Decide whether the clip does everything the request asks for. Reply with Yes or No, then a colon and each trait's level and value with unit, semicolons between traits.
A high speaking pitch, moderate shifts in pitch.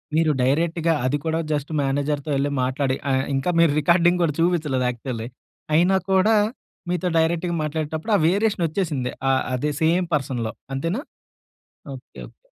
No: medium, 155 Hz; average, 4.2 semitones